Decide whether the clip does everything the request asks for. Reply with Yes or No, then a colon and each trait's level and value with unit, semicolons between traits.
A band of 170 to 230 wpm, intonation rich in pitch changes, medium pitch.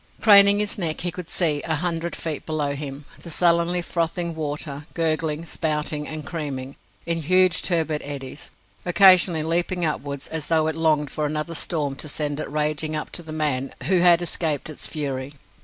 No: average, 175 wpm; narrow, 2.4 semitones; medium, 155 Hz